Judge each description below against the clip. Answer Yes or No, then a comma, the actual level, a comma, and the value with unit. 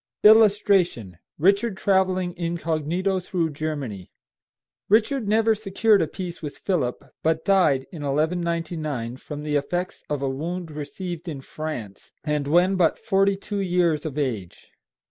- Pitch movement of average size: Yes, average, 4.3 semitones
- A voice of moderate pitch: Yes, medium, 170 Hz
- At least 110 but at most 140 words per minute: Yes, slow, 135 wpm